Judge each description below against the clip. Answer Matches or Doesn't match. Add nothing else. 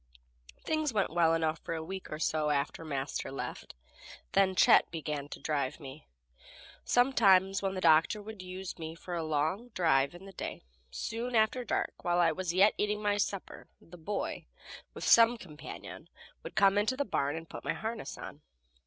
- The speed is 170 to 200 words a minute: Matches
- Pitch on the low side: Doesn't match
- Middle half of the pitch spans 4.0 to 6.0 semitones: Matches